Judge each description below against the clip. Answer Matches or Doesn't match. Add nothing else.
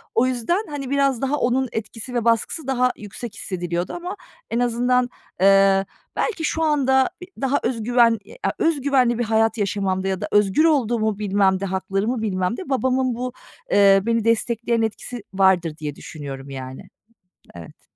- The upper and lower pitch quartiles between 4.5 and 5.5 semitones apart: Matches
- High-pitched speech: Matches